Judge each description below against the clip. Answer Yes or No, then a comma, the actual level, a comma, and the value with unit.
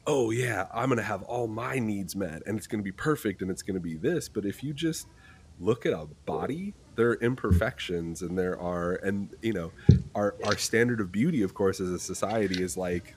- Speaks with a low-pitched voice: Yes, low, 100 Hz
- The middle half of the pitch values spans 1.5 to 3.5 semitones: No, average, 4.1 semitones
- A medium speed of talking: No, fast, 220 wpm